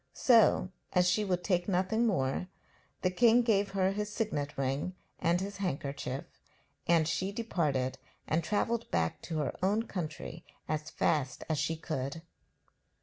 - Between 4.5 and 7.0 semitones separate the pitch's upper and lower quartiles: Yes, average, 4.8 semitones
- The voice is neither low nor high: Yes, medium, 180 Hz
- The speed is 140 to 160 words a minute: Yes, average, 145 wpm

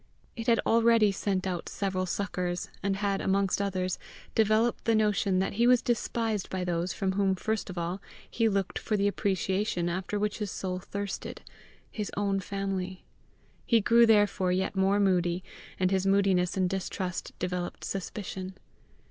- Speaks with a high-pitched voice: Yes, high, 195 Hz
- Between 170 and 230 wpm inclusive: No, average, 160 wpm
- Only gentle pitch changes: Yes, narrow, 2.0 semitones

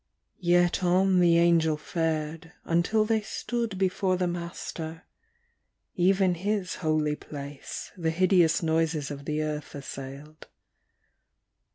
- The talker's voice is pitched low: No, medium, 170 Hz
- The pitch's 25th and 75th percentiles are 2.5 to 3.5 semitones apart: Yes, average, 3.0 semitones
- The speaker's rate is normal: No, slow, 110 wpm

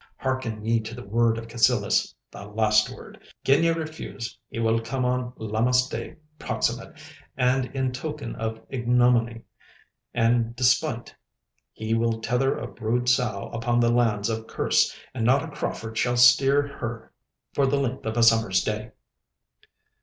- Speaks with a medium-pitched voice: No, low, 120 Hz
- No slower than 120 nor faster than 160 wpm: Yes, average, 150 wpm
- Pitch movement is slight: Yes, narrow, 2.0 semitones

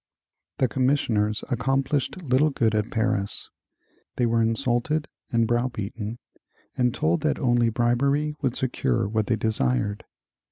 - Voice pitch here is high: No, low, 120 Hz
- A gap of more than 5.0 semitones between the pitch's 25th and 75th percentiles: No, average, 3.2 semitones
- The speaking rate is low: Yes, slow, 125 wpm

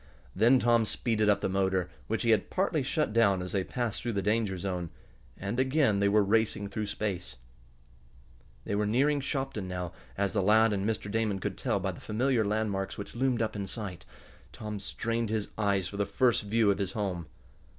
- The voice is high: No, low, 105 Hz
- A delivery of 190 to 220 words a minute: Yes, average, 200 wpm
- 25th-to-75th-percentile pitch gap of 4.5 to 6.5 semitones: No, average, 2.7 semitones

